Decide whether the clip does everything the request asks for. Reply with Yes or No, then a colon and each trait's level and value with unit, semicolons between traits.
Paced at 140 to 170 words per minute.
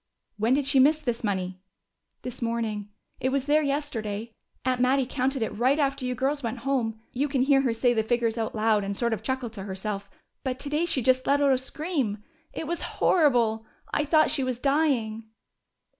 No: average, 200 wpm